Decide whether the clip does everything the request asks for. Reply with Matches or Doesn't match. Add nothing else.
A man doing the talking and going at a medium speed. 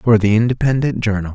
Matches